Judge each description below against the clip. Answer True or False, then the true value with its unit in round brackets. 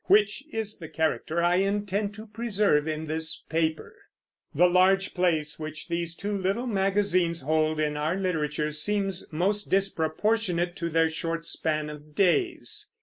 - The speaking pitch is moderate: True (175 Hz)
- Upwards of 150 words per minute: False (145 wpm)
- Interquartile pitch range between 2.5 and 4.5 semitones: True (4.0 semitones)